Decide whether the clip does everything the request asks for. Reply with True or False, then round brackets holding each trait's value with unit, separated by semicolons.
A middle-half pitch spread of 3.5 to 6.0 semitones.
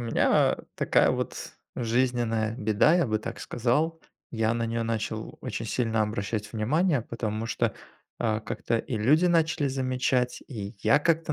True (3.8 semitones)